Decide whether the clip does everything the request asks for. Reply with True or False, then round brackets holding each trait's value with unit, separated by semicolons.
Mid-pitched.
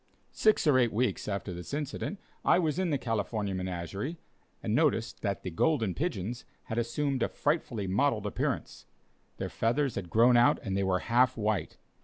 False (115 Hz)